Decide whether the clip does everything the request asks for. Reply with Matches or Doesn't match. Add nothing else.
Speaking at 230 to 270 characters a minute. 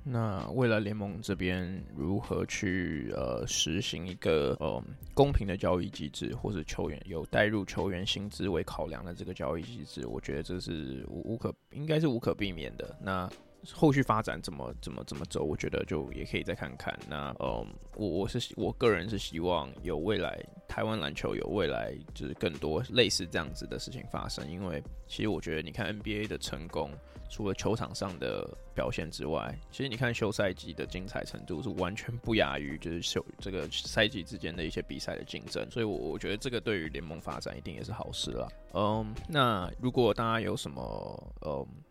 Doesn't match